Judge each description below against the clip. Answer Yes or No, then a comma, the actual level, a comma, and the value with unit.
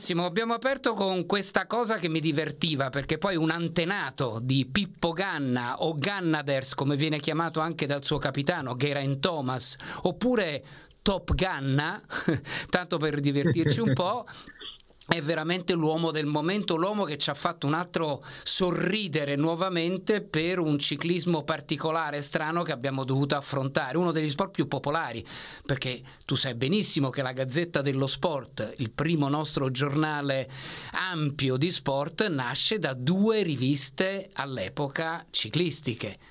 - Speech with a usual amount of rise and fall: Yes, average, 3.9 semitones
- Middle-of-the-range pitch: Yes, medium, 155 Hz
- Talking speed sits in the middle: Yes, average, 140 wpm